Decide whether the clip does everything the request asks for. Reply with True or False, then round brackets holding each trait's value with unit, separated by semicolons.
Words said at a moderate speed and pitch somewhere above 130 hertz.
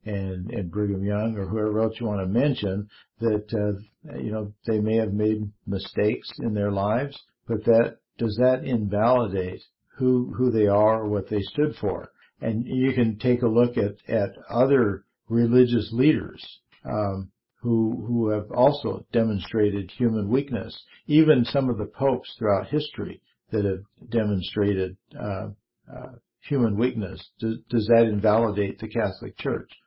False (155 wpm; 110 Hz)